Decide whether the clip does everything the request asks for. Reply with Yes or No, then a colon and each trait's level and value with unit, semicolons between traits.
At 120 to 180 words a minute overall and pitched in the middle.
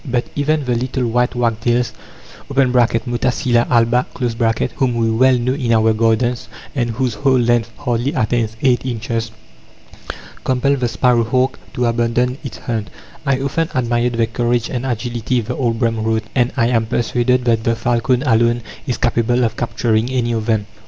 No: average, 165 wpm; low, 120 Hz